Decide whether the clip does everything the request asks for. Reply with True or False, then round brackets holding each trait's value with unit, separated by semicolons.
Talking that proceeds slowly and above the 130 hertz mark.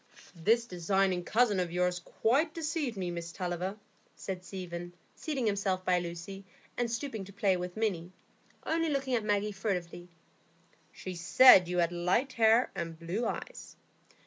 False (150 wpm; 190 Hz)